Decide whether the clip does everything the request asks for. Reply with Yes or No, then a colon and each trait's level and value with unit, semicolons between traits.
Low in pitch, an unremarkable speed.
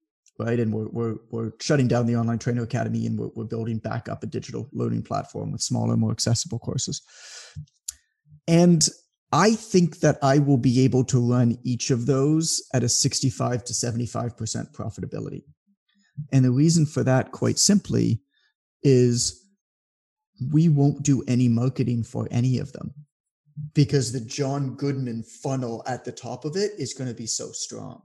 Yes: low, 130 Hz; average, 165 wpm